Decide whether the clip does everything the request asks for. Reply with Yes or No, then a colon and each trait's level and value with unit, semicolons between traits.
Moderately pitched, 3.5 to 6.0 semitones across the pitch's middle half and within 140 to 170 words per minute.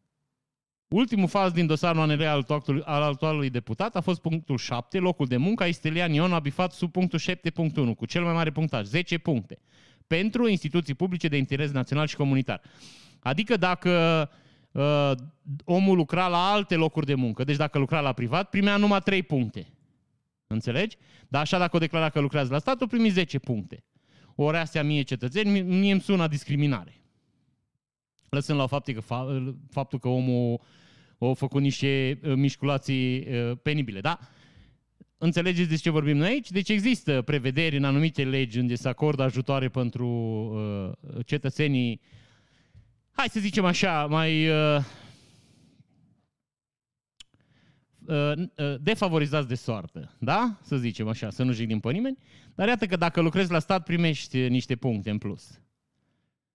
Yes: medium, 145 Hz; average, 4.7 semitones; average, 150 wpm